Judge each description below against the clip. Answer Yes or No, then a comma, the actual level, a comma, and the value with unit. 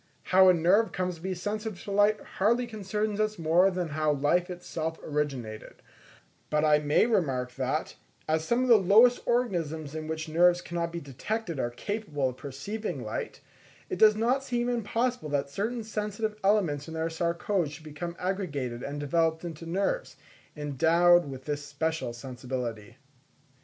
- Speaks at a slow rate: No, average, 160 wpm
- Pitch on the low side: No, medium, 170 Hz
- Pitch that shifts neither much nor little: No, wide, 6.0 semitones